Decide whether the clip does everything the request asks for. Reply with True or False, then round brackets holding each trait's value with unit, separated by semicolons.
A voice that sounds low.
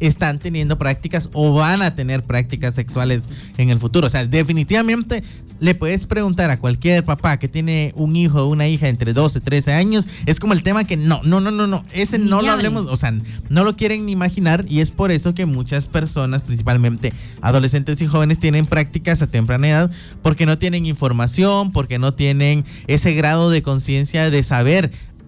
False (155 Hz)